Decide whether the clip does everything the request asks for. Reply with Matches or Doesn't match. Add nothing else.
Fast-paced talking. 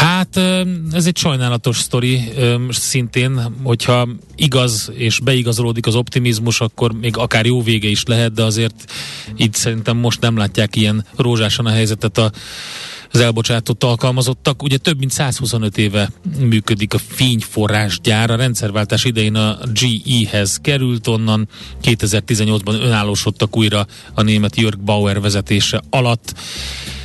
Doesn't match